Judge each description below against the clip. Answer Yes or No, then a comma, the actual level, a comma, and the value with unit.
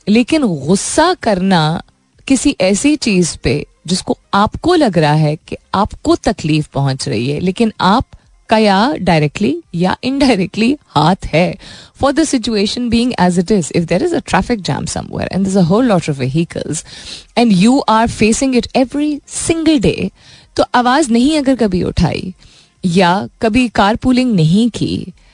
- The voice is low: No, high, 215 Hz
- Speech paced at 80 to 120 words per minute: No, average, 160 wpm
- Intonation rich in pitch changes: Yes, wide, 6.5 semitones